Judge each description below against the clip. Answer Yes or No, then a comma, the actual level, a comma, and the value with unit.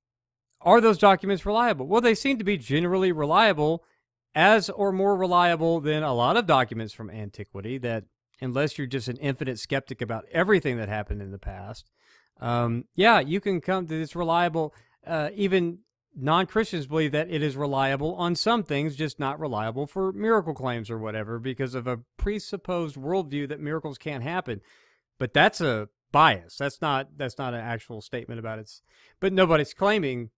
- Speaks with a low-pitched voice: No, medium, 150 Hz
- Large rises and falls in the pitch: Yes, wide, 7.0 semitones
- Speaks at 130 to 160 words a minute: No, average, 175 wpm